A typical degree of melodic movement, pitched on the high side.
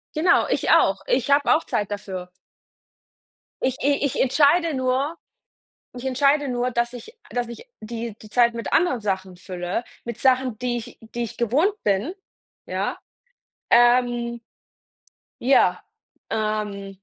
Yes: average, 3.8 semitones; high, 240 Hz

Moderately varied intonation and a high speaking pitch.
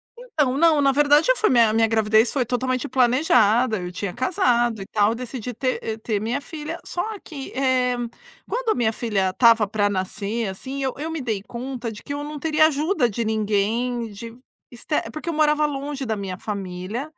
Yes: average, 4.8 semitones; high, 245 Hz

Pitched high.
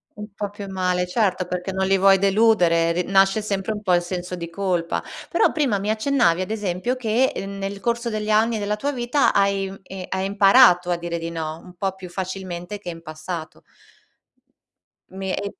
Yes: high, 195 Hz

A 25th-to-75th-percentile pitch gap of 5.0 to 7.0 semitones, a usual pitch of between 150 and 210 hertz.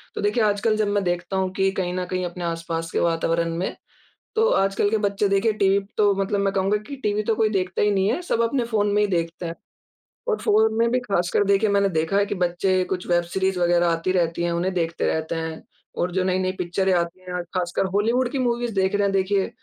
No: average, 2.9 semitones; high, 190 Hz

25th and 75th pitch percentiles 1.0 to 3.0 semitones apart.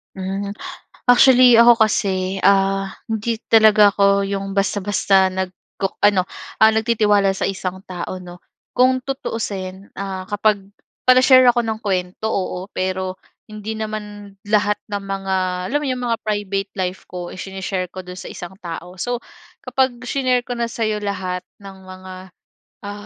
Yes: average, 2.7 semitones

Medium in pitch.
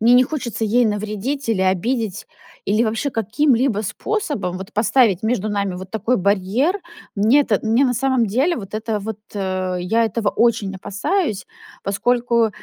No: high, 220 Hz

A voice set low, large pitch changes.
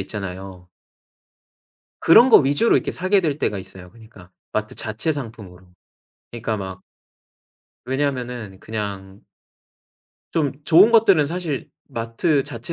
Yes: low, 115 Hz; wide, 7.5 semitones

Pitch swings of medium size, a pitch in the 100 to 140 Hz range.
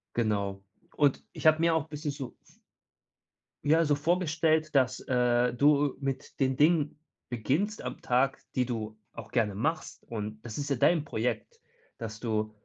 Yes: average, 5.0 semitones; low, 135 Hz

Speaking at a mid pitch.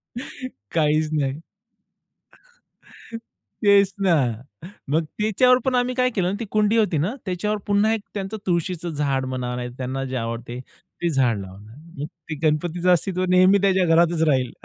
Yes: medium, 170 Hz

